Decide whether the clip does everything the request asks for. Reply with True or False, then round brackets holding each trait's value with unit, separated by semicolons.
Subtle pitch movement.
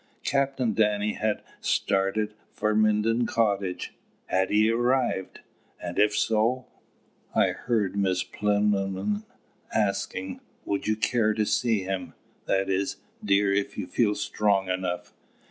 True (2.0 semitones)